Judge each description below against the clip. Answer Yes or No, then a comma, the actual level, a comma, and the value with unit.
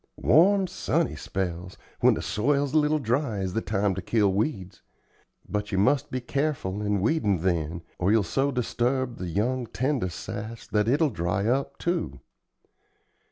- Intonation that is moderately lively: No, wide, 6.4 semitones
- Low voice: Yes, low, 110 Hz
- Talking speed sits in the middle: Yes, average, 160 wpm